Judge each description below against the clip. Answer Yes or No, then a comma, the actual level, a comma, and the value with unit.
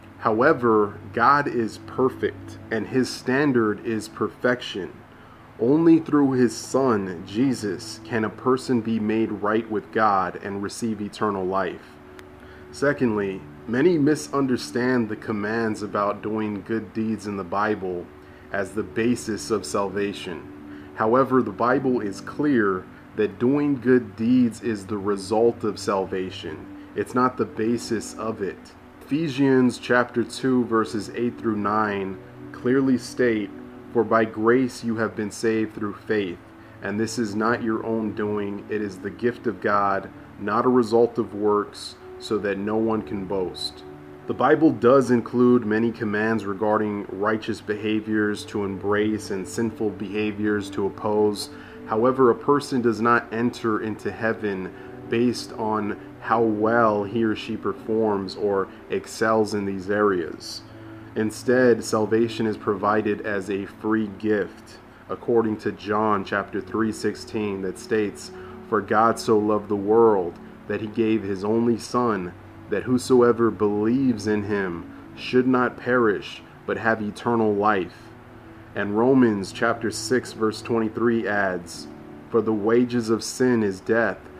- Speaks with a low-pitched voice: Yes, low, 110 Hz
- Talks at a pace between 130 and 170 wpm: Yes, average, 140 wpm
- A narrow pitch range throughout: Yes, narrow, 2.3 semitones